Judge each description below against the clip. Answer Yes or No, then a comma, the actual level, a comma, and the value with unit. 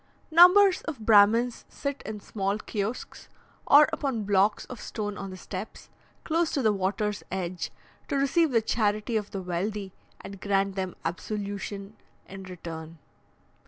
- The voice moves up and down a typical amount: Yes, average, 3.5 semitones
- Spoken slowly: No, average, 145 wpm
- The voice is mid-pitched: No, high, 205 Hz